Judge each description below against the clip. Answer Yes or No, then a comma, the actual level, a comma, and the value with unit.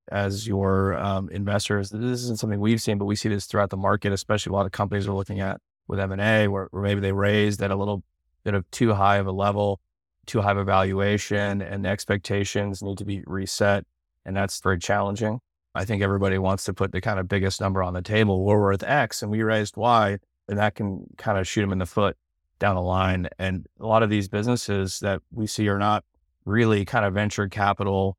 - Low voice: Yes, low, 100 Hz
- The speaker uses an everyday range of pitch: No, narrow, 1.4 semitones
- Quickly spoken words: Yes, fast, 230 wpm